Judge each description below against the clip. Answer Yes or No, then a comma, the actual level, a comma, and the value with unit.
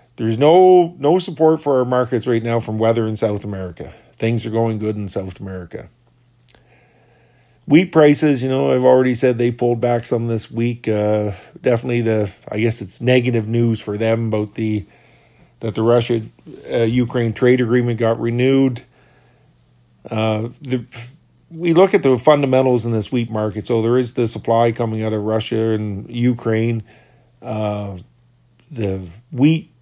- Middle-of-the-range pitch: No, low, 115 Hz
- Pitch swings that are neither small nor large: No, narrow, 2.3 semitones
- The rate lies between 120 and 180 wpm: Yes, average, 160 wpm